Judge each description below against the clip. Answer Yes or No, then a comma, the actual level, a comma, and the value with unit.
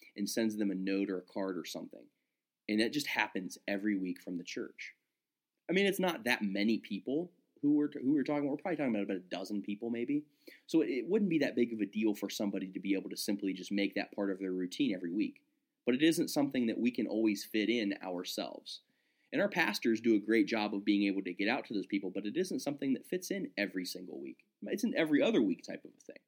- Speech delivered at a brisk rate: Yes, fast, 255 wpm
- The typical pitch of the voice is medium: No, low, 105 Hz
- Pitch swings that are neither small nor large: No, wide, 7.0 semitones